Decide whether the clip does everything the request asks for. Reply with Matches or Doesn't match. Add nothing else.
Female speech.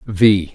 Doesn't match